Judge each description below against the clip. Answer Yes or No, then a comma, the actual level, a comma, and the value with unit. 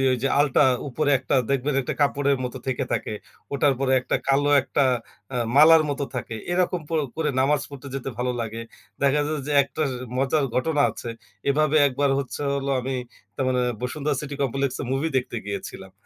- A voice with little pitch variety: Yes, narrow, 2.3 semitones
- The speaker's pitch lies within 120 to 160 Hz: Yes, medium, 140 Hz